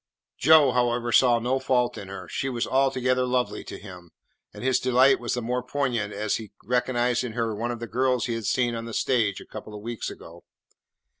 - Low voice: Yes, low, 120 Hz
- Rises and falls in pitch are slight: Yes, narrow, 2.0 semitones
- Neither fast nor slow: No, fast, 215 wpm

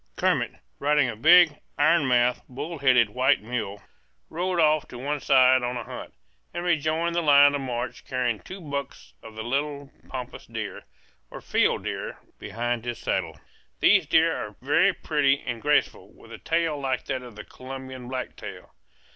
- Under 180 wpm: Yes, average, 170 wpm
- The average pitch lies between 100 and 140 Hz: Yes, low, 135 Hz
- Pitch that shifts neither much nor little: Yes, average, 3.4 semitones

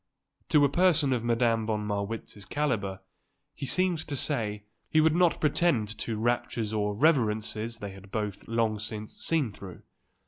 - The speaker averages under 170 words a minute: Yes, average, 160 wpm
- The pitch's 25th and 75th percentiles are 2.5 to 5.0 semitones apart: No, wide, 5.4 semitones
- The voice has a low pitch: Yes, low, 115 Hz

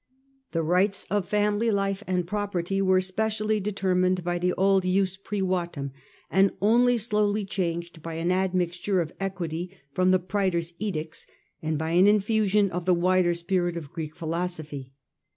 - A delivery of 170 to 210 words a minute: No, average, 155 wpm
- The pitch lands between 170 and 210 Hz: Yes, medium, 185 Hz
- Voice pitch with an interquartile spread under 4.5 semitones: Yes, narrow, 2.6 semitones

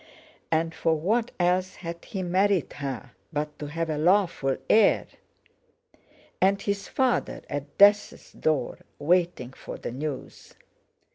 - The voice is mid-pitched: Yes, medium, 170 Hz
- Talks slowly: Yes, slow, 125 wpm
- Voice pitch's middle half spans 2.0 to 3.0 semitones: No, average, 4.6 semitones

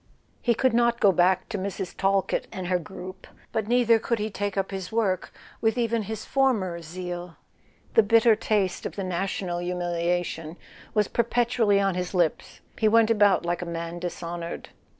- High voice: Yes, high, 195 Hz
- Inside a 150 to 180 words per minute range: Yes, average, 170 wpm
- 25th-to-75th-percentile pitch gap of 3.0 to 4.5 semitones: Yes, average, 3.9 semitones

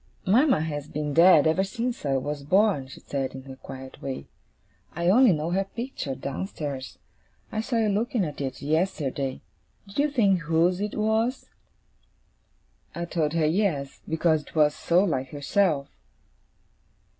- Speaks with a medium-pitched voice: Yes, medium, 165 Hz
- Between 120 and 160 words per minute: Yes, average, 155 wpm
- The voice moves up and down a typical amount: No, wide, 6.0 semitones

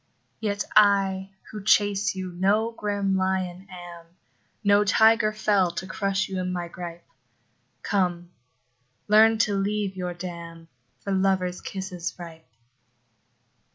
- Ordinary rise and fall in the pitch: No, narrow, 2.3 semitones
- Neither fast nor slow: No, slow, 120 wpm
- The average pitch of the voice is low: No, high, 190 Hz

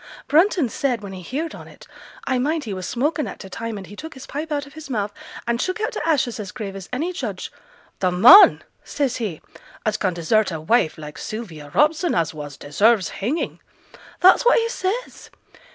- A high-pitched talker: Yes, high, 235 Hz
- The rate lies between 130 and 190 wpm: No, fast, 205 wpm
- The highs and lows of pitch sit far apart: Yes, wide, 8.3 semitones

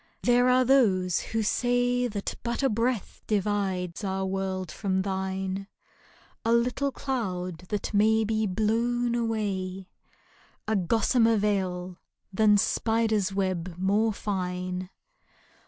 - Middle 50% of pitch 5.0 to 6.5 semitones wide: No, average, 3.4 semitones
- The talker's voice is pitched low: No, high, 205 Hz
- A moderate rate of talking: No, slow, 120 wpm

